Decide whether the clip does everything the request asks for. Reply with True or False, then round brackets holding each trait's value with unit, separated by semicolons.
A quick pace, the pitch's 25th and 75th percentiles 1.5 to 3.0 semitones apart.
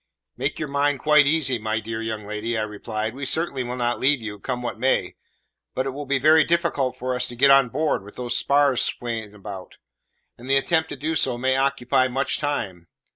False (215 wpm; 3.9 semitones)